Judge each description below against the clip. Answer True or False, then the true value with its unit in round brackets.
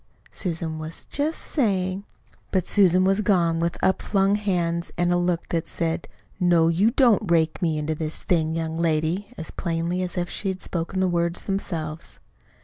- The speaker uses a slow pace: False (175 wpm)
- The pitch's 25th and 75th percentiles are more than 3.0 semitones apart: False (2.5 semitones)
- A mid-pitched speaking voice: True (175 Hz)